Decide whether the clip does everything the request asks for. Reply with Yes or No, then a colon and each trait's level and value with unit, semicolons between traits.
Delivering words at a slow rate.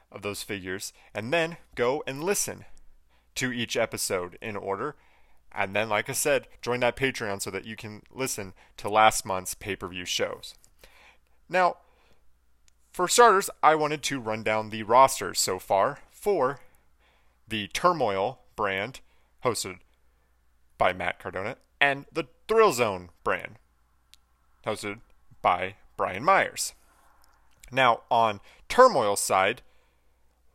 Yes: slow, 125 wpm